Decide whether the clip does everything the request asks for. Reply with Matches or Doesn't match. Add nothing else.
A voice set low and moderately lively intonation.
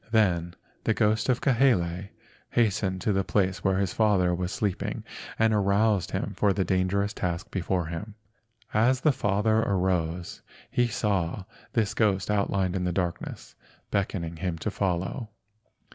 Matches